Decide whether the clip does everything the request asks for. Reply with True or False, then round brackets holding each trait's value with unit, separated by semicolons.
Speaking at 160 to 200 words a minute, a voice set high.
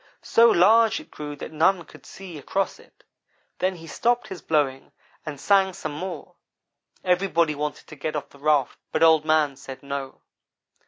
False (170 wpm; 155 Hz)